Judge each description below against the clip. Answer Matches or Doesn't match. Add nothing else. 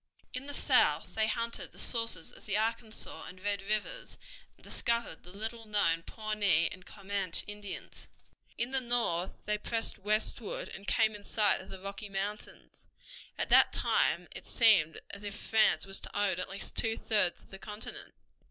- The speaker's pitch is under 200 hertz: Doesn't match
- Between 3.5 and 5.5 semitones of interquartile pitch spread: Doesn't match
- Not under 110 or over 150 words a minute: Doesn't match